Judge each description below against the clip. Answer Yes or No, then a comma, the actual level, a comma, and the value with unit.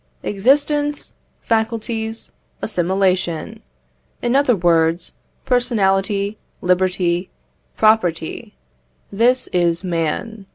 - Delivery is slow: Yes, slow, 70 wpm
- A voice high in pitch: Yes, high, 195 Hz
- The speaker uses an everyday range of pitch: Yes, average, 4.5 semitones